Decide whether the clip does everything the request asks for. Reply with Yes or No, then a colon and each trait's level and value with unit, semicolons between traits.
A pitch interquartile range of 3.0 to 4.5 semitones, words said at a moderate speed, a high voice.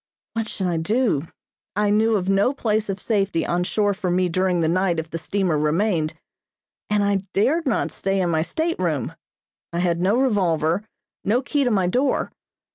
Yes: average, 3.8 semitones; average, 185 wpm; high, 195 Hz